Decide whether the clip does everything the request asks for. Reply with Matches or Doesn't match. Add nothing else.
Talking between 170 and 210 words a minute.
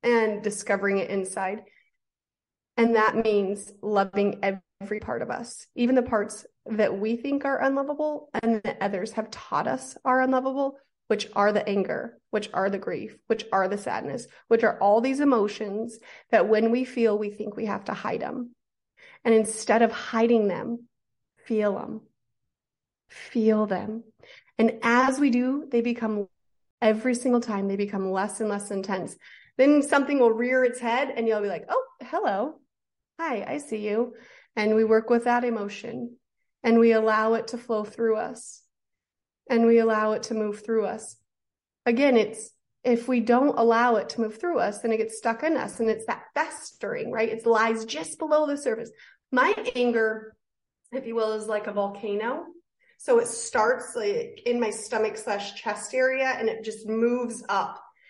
Matches